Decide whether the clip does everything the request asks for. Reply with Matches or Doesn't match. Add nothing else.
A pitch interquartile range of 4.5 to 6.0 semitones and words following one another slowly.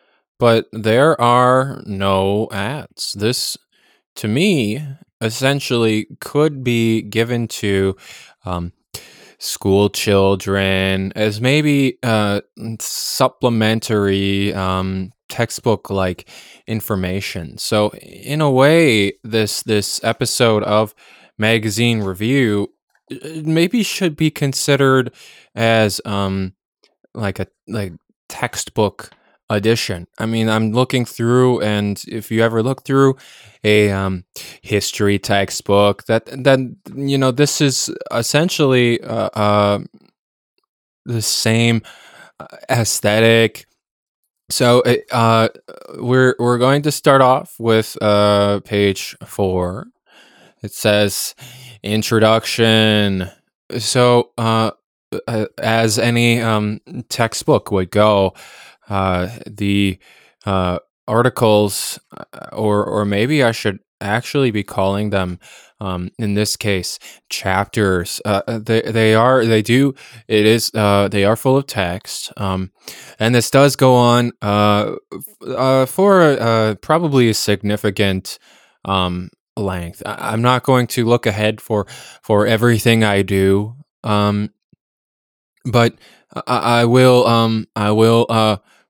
Doesn't match